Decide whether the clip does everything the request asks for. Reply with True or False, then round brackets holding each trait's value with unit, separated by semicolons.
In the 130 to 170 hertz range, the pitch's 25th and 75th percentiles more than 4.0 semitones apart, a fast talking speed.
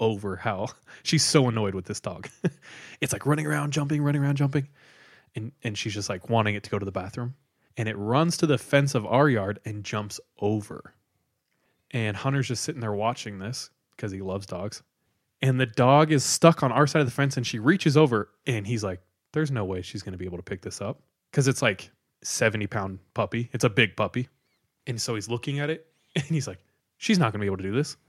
False (120 Hz; 5.4 semitones; 225 wpm)